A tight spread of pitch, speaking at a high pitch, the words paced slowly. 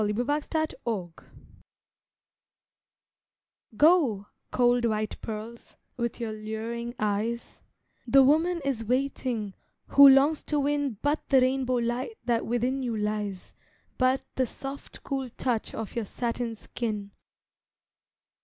No: average, 3.7 semitones; high, 240 Hz; slow, 115 wpm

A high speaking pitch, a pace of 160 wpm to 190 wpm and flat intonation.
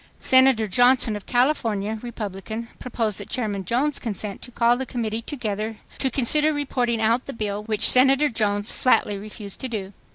No: high, 230 Hz; average, 165 wpm; average, 3.3 semitones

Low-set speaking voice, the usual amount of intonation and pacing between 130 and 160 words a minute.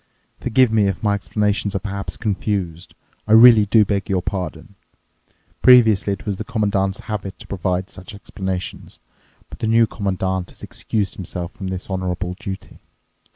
No: low, 100 Hz; narrow, 2.3 semitones; average, 155 wpm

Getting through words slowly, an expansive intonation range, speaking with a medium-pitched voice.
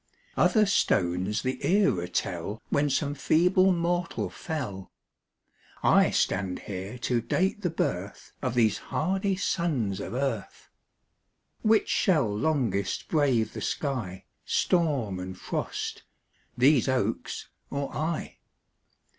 No: slow, 115 wpm; wide, 8.6 semitones; low, 130 Hz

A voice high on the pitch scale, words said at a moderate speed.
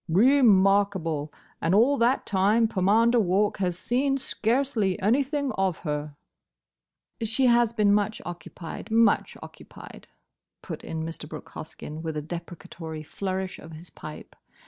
No: high, 195 Hz; slow, 130 wpm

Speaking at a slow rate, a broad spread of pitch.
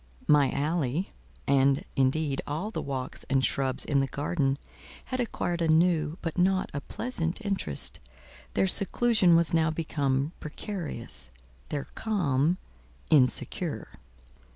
No: slow, 120 wpm; average, 4.4 semitones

